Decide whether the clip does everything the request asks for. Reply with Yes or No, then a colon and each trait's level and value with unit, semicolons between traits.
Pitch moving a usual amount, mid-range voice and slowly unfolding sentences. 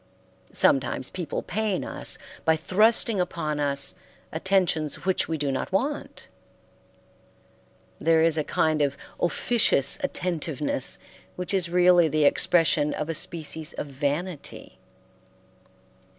Yes: average, 3.6 semitones; medium, 160 Hz; slow, 115 wpm